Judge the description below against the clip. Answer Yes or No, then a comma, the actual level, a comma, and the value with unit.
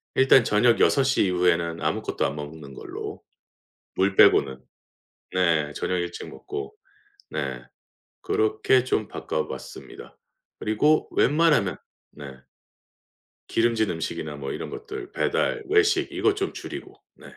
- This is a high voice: No, low, 110 Hz